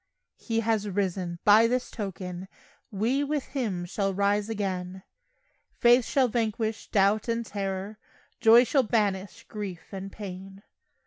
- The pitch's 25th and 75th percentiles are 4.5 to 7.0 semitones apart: No, average, 3.0 semitones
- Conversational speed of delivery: No, slow, 130 wpm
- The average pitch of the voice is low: No, high, 205 Hz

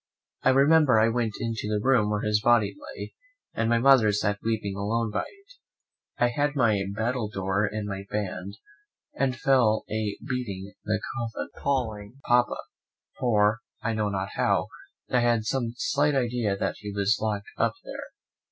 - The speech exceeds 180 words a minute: No, average, 165 wpm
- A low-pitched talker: Yes, low, 110 Hz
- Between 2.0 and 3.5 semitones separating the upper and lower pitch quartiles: Yes, average, 2.9 semitones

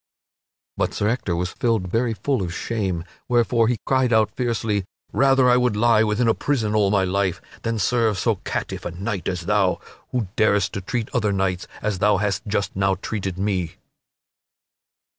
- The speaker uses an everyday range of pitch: Yes, average, 3.3 semitones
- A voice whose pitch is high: No, low, 105 Hz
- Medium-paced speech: Yes, average, 180 wpm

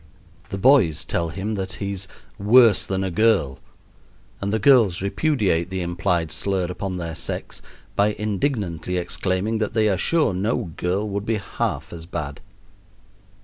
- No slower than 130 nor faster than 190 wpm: Yes, average, 150 wpm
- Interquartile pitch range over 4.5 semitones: No, average, 3.4 semitones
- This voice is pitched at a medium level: No, very low, 95 Hz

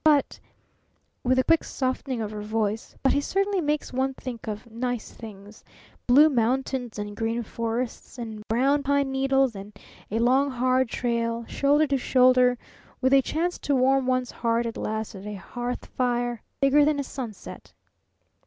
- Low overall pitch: No, very high, 250 Hz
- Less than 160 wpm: No, average, 170 wpm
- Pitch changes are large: No, average, 3.0 semitones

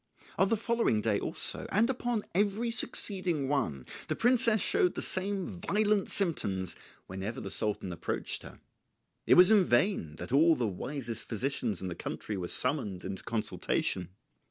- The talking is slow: No, average, 155 wpm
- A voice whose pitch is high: No, medium, 145 Hz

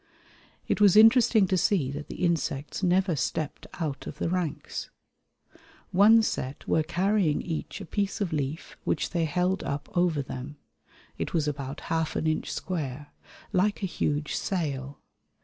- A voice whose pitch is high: No, medium, 165 Hz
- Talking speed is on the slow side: No, average, 155 wpm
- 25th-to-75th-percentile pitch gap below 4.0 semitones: No, average, 4.4 semitones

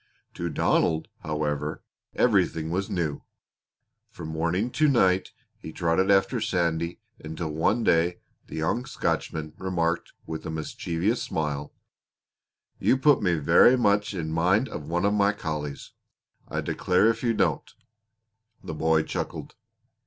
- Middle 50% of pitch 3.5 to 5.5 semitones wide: Yes, average, 4.2 semitones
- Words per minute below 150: Yes, slow, 135 wpm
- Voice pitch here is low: Yes, very low, 85 Hz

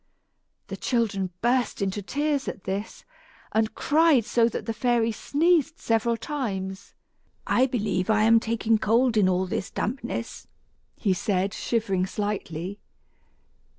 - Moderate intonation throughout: Yes, average, 3.7 semitones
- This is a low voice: No, high, 225 Hz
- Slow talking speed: Yes, slow, 130 wpm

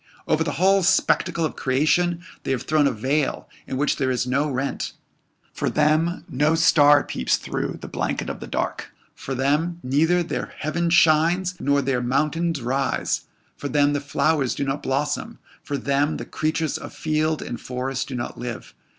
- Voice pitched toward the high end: No, medium, 145 Hz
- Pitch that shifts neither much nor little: Yes, average, 3.2 semitones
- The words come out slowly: No, average, 175 wpm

